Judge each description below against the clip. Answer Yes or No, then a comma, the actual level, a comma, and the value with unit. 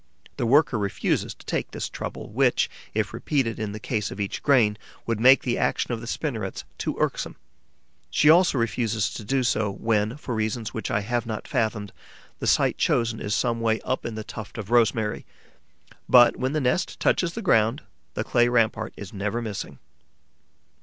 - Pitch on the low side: Yes, low, 115 Hz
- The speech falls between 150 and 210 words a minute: Yes, average, 185 wpm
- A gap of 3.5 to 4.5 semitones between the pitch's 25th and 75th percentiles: No, narrow, 2.5 semitones